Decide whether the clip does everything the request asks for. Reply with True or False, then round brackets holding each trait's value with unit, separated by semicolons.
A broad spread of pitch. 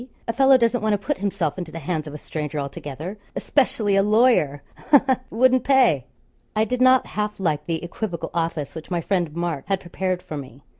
True (6.3 semitones)